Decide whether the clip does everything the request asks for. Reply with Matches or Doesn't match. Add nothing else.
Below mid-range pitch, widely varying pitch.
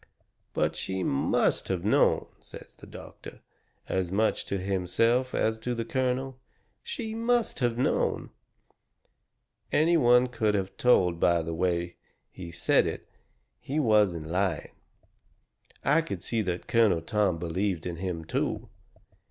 Matches